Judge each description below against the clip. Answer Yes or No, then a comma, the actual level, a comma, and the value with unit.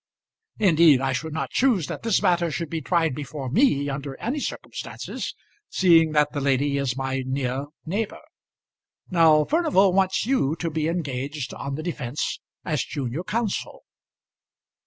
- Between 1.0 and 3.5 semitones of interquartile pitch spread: No, average, 4.5 semitones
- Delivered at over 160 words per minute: No, average, 150 wpm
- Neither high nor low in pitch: Yes, medium, 155 Hz